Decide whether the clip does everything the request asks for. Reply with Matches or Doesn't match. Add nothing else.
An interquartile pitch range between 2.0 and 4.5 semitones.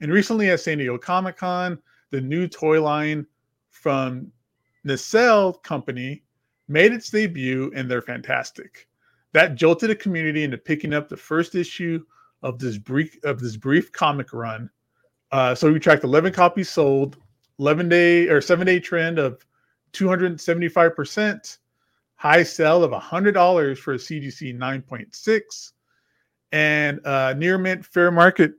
Doesn't match